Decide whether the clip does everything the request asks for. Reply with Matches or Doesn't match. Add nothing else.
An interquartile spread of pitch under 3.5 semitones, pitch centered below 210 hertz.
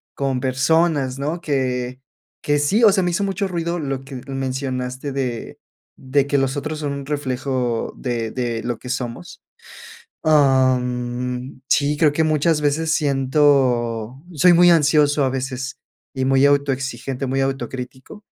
Matches